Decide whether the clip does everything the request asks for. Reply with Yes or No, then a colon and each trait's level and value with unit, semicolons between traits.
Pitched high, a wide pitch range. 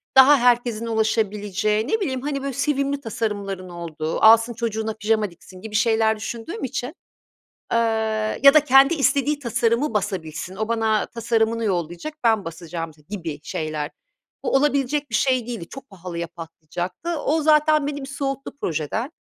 Yes: high, 225 Hz; wide, 6.2 semitones